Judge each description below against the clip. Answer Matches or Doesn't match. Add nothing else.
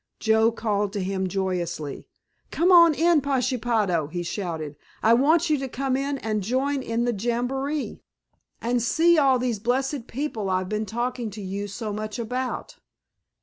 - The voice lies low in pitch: Doesn't match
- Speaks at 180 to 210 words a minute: Doesn't match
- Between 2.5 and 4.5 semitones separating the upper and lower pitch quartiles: Doesn't match